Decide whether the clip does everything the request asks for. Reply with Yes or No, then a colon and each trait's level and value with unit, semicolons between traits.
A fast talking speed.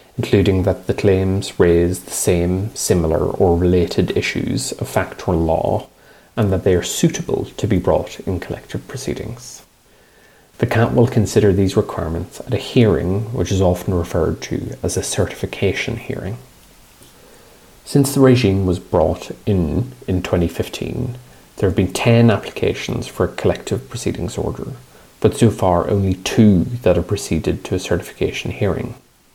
No: average, 150 wpm